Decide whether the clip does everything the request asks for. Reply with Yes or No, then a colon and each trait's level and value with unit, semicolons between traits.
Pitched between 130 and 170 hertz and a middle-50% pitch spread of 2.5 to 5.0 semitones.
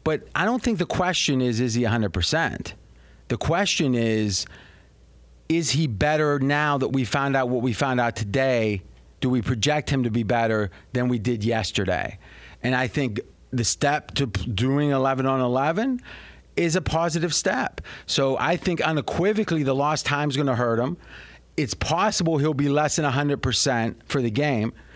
Yes: low, 135 Hz; average, 4.5 semitones